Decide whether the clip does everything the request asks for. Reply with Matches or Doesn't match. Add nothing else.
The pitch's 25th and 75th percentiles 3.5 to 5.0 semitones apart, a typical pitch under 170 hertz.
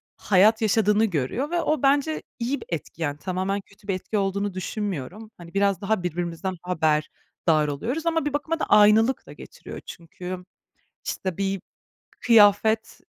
Doesn't match